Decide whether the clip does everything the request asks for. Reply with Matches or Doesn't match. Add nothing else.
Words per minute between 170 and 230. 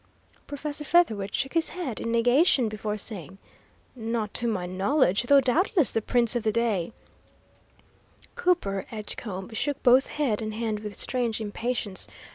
Doesn't match